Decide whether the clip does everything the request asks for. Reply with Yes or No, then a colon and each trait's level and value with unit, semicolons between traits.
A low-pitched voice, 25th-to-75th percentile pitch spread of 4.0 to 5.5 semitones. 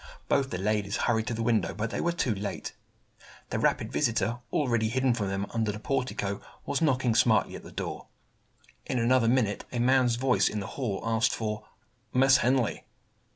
No: low, 115 Hz; average, 3.1 semitones